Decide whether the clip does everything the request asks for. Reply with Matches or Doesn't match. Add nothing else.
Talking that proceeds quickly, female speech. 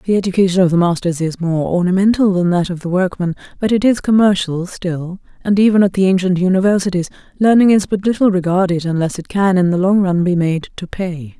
Matches